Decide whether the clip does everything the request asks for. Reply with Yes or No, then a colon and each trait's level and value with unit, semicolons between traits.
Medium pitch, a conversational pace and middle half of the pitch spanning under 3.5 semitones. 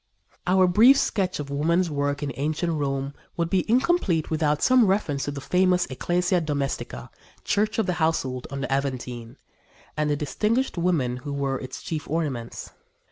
No: medium, 155 Hz; average, 170 wpm; average, 4.7 semitones